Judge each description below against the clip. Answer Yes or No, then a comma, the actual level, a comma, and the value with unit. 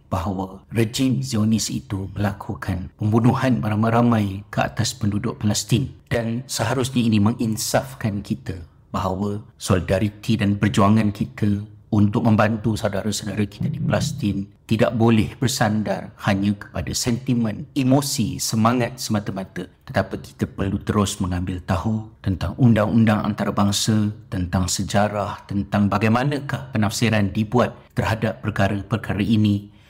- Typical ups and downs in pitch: No, narrow, 2.3 semitones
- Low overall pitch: Yes, low, 110 Hz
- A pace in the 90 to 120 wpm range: Yes, average, 110 wpm